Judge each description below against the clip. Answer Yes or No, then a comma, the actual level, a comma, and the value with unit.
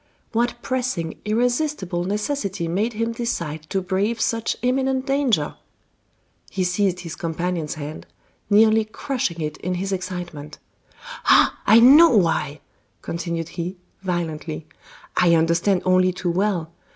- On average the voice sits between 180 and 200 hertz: Yes, medium, 185 Hz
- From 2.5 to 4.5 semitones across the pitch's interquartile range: No, average, 5.2 semitones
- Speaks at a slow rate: Yes, slow, 125 wpm